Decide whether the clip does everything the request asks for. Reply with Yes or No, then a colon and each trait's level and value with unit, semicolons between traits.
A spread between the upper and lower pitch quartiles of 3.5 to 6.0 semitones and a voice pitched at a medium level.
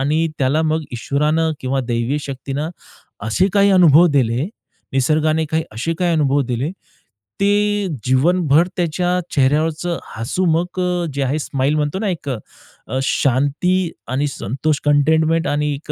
Yes: average, 3.8 semitones; medium, 150 Hz